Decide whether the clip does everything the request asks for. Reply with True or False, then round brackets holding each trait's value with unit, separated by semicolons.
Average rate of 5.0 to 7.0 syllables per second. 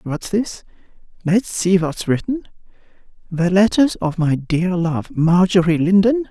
False (4.0 syllables/s)